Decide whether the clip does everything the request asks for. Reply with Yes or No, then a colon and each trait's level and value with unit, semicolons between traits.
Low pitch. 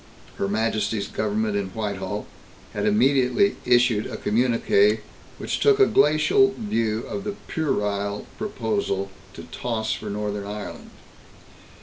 Yes: low, 110 Hz